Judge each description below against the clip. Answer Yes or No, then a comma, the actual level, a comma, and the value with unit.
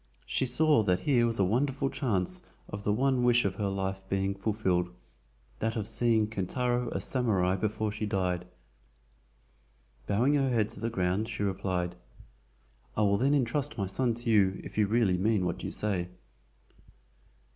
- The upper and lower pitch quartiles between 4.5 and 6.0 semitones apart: No, average, 3.9 semitones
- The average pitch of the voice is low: Yes, low, 105 Hz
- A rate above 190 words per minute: No, average, 165 wpm